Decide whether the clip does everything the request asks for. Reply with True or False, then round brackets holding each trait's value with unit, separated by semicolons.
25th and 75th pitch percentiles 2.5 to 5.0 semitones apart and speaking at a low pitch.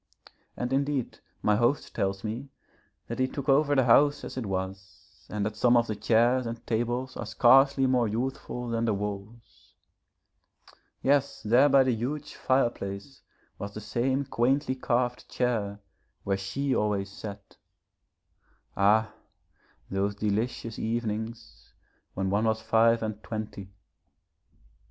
True (3.8 semitones; 115 Hz)